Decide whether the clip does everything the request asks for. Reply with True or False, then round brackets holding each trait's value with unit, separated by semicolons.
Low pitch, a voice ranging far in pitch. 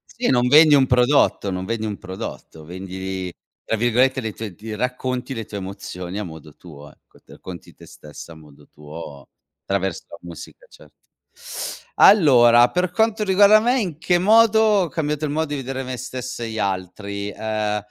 True (115 Hz; 7.8 semitones)